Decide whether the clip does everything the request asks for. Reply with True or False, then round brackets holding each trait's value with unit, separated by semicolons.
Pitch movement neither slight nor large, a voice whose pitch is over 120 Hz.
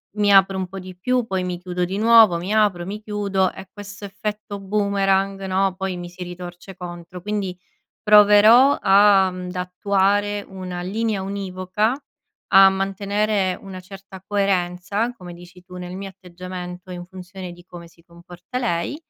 False (2.2 semitones; 190 Hz)